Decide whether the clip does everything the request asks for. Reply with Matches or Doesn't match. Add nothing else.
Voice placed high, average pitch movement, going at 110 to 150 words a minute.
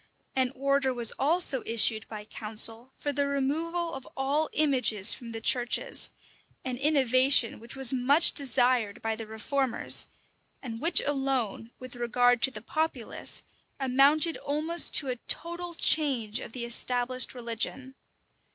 Matches